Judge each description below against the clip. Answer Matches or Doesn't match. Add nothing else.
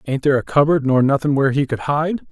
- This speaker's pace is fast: Matches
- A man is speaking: Matches